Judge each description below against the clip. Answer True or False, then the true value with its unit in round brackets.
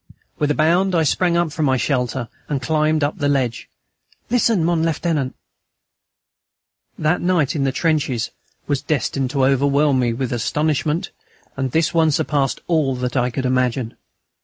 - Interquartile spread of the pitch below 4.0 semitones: True (3.5 semitones)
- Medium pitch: True (145 Hz)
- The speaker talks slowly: False (155 wpm)